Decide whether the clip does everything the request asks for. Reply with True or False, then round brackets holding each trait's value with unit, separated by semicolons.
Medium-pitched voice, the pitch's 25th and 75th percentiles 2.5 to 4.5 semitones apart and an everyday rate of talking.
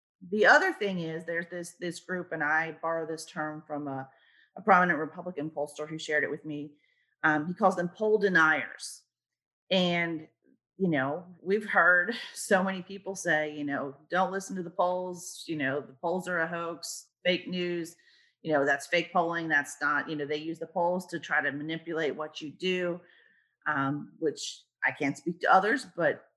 True (170 Hz; 2.9 semitones; 190 wpm)